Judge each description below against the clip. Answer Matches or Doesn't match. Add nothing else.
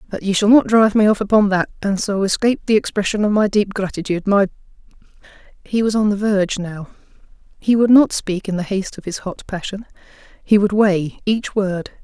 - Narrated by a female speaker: Matches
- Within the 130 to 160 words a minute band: Doesn't match